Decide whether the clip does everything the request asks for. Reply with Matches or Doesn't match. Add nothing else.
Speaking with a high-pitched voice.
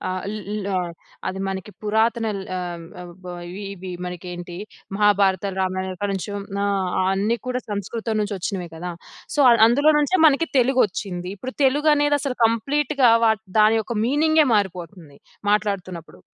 Matches